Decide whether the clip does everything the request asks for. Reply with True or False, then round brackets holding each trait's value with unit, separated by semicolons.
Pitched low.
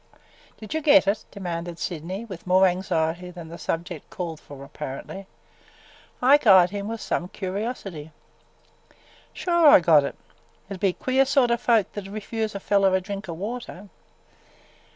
False (190 Hz)